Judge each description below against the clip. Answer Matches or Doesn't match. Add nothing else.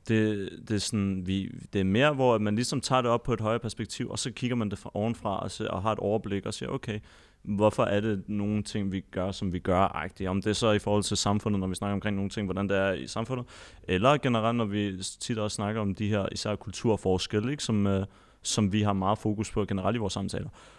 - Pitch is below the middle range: Matches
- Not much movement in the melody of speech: Matches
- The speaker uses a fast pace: Matches